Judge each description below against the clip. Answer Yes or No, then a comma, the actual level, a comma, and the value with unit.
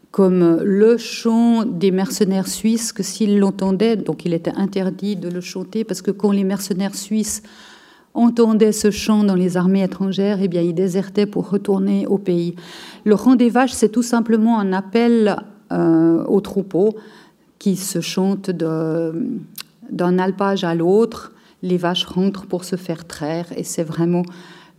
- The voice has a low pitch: No, high, 195 Hz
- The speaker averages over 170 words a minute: No, average, 160 wpm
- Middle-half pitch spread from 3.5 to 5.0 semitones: No, average, 3.0 semitones